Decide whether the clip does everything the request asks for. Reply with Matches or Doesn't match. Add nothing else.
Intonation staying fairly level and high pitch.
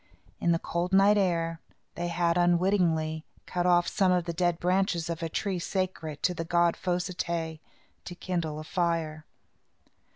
Doesn't match